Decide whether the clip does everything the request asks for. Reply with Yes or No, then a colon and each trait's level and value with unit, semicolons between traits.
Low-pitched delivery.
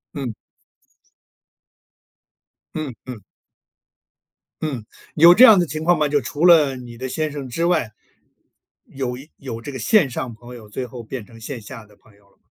Yes: low, 130 Hz